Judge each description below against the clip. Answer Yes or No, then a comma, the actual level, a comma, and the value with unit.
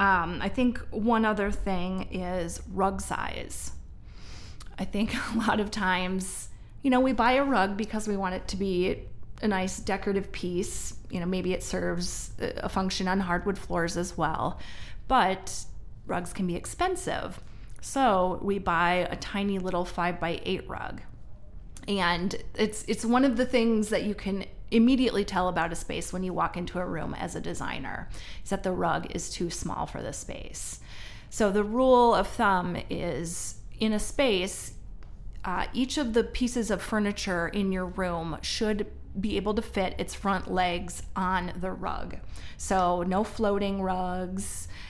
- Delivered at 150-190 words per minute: Yes, average, 165 wpm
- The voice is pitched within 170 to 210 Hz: Yes, high, 190 Hz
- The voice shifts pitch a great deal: No, average, 3.1 semitones